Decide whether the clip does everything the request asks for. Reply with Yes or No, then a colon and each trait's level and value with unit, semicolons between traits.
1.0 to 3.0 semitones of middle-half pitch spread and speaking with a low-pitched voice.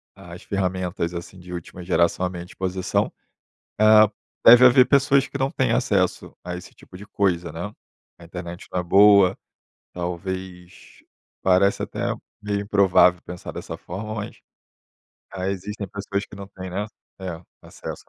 Yes: narrow, 2.4 semitones; very low, 95 Hz